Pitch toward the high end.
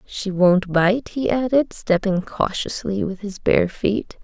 Yes: high, 200 Hz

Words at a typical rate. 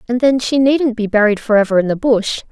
No: fast, 265 wpm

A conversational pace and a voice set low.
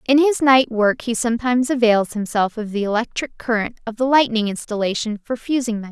No: average, 195 wpm; high, 230 Hz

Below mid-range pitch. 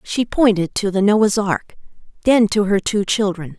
No: high, 205 Hz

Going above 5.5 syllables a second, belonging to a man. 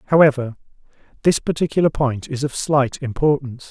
Yes: 5.7 syllables/s; male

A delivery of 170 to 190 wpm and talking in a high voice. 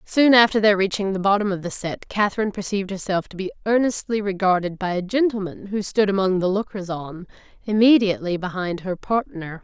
Yes: average, 180 wpm; high, 195 Hz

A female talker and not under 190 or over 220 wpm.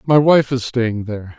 No: male; fast, 215 wpm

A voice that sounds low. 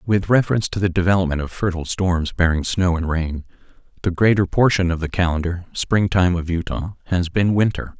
Yes: very low, 90 Hz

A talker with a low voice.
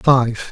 Yes: low, 125 Hz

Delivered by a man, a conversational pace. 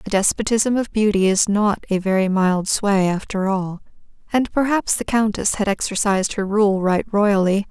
No: female; average, 170 wpm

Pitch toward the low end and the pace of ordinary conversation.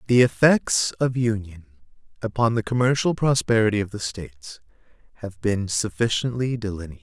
No: low, 110 Hz; slow, 130 wpm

